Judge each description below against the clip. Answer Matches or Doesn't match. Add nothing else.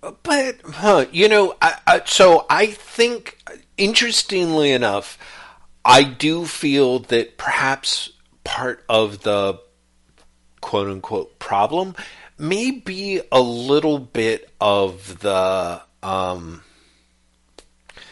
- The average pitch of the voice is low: Matches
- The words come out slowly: Matches